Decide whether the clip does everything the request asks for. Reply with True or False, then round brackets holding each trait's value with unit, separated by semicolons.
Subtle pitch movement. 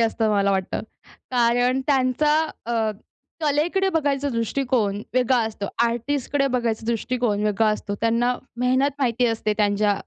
False (3.3 semitones)